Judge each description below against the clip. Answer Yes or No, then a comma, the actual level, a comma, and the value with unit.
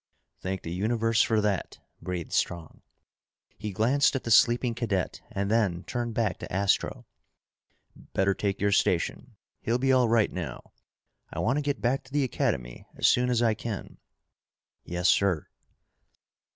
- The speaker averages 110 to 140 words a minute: No, average, 155 wpm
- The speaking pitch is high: No, low, 110 Hz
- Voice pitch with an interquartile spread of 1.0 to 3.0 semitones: No, average, 4.1 semitones